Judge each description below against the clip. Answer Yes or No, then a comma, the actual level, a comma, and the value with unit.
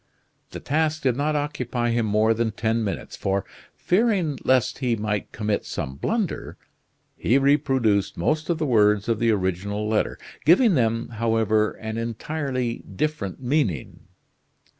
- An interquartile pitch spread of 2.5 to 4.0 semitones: No, average, 5.3 semitones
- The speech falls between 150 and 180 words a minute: No, average, 140 wpm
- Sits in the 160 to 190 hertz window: No, low, 115 Hz